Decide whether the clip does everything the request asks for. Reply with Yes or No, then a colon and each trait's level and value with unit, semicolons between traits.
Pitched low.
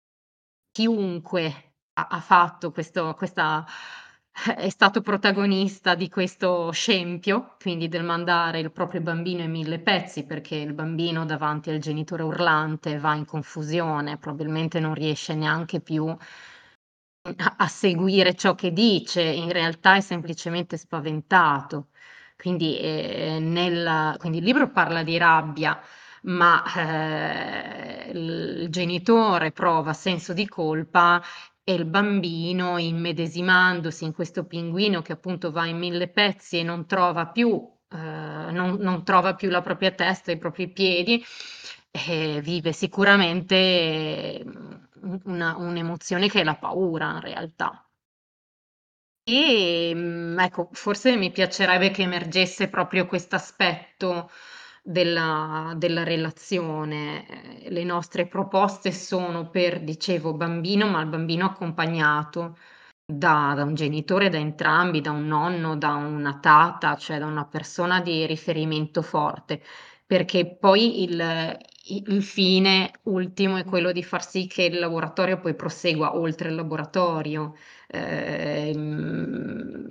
No: medium, 175 Hz